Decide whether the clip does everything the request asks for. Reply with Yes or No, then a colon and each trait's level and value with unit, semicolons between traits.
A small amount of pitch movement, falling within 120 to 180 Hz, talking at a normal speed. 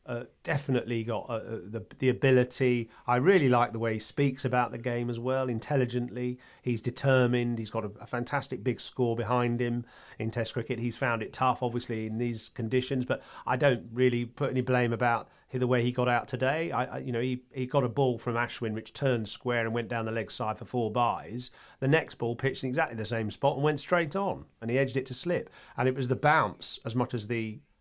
No: narrow, 1.8 semitones; low, 125 Hz; fast, 230 wpm